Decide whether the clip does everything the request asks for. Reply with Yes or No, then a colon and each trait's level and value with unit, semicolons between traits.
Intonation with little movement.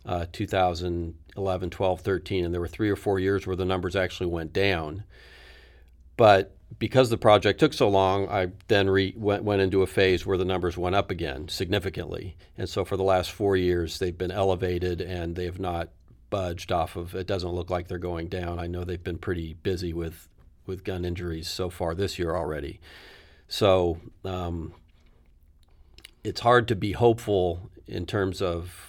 Yes: narrow, 2.1 semitones